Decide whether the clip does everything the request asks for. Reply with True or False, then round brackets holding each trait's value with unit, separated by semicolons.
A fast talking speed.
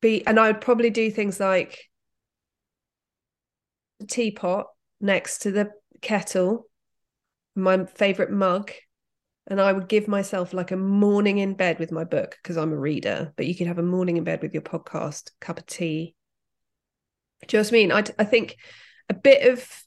False (180 wpm)